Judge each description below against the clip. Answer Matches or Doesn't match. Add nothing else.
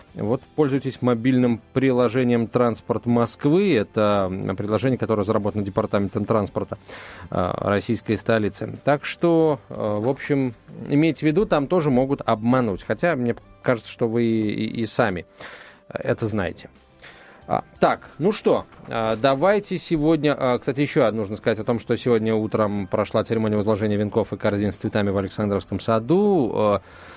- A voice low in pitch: Matches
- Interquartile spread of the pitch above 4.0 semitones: Doesn't match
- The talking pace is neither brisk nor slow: Matches